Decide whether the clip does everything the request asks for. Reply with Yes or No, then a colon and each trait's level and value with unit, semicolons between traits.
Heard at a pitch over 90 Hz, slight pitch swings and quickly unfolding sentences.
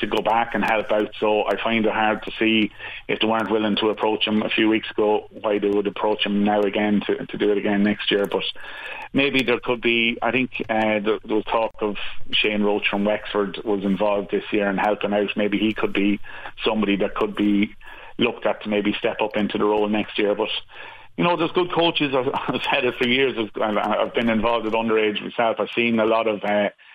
Yes: low, 105 Hz; narrow, 1.4 semitones; fast, 230 wpm